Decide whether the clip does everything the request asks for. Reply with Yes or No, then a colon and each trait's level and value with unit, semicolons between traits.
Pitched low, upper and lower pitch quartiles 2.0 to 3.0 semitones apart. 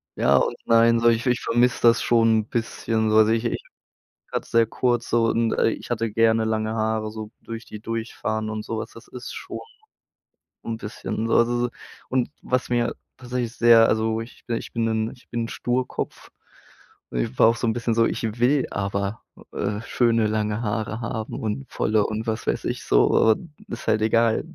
No: low, 115 Hz; narrow, 1.3 semitones